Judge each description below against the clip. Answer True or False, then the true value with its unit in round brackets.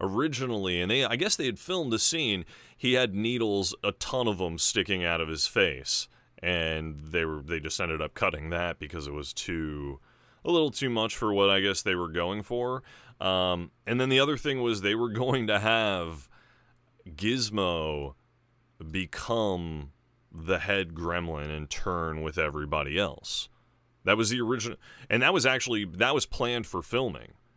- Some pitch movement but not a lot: False (6.4 semitones)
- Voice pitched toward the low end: True (100 Hz)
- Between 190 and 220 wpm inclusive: False (175 wpm)